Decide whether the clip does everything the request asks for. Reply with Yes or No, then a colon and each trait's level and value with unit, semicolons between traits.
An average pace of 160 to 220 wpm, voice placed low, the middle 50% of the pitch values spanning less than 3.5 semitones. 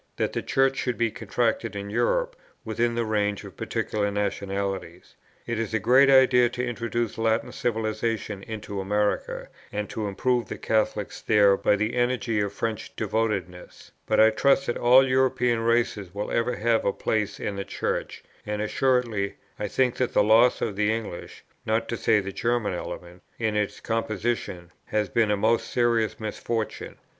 Yes: average, 170 wpm; low, 110 Hz; narrow, 2.5 semitones